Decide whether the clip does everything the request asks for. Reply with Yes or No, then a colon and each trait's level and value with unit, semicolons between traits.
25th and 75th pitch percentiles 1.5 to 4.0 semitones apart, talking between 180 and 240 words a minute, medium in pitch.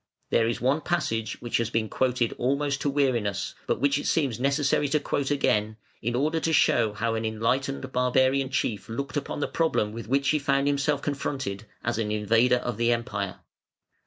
No: average, 3.7 semitones; average, 190 wpm; low, 125 Hz